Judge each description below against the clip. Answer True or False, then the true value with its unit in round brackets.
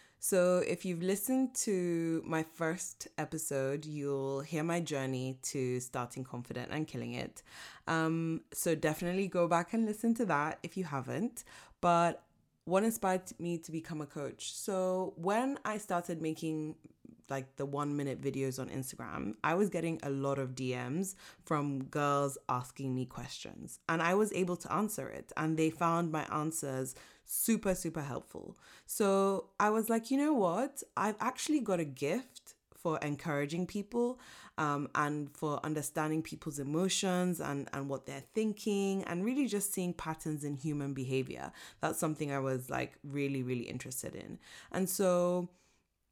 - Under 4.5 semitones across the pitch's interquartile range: False (5.0 semitones)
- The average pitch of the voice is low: False (160 Hz)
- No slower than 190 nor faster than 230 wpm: False (160 wpm)